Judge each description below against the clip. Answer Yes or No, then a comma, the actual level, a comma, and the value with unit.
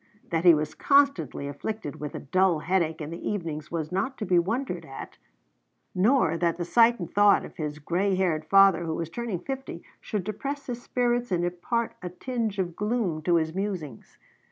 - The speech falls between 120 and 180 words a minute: No, average, 190 wpm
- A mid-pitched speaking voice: Yes, medium, 180 Hz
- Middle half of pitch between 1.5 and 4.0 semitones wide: No, average, 5.3 semitones